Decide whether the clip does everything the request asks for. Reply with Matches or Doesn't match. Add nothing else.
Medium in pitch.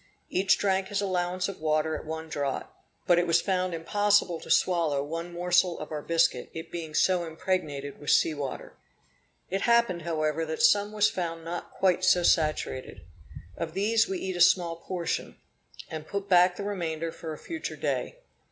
Matches